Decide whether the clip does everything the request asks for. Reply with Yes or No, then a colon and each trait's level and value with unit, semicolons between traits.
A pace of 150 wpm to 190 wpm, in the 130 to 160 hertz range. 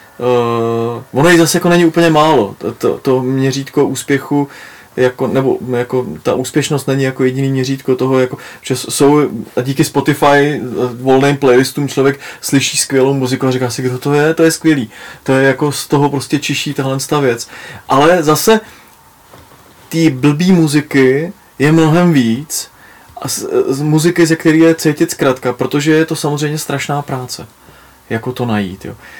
Yes: average, 165 wpm; medium, 140 Hz